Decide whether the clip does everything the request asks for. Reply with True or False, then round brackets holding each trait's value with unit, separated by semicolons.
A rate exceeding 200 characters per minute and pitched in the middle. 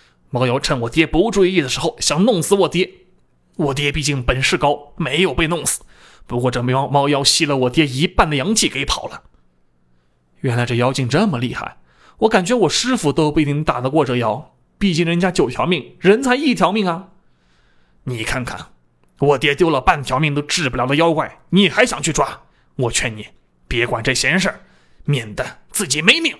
True (275 characters per minute; 145 Hz)